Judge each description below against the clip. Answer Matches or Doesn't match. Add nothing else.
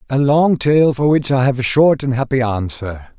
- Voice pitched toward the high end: Doesn't match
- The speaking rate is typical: Doesn't match